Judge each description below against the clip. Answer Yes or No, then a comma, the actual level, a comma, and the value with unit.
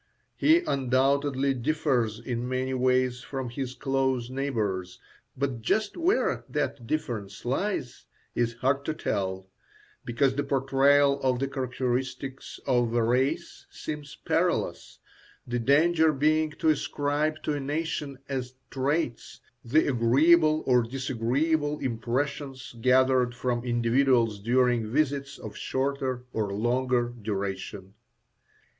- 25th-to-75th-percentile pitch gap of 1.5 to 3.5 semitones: Yes, average, 2.8 semitones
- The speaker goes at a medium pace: No, slow, 115 wpm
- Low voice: Yes, low, 130 Hz